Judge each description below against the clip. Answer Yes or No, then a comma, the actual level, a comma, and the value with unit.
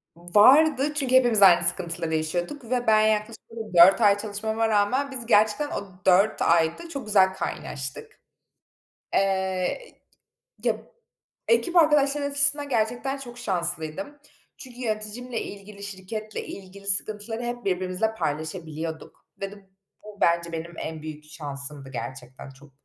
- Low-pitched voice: No, high, 205 Hz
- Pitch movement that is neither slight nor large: No, wide, 6.0 semitones